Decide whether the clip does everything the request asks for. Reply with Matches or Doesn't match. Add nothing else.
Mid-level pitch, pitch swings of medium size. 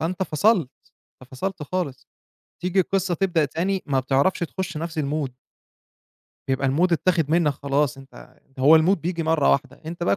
Matches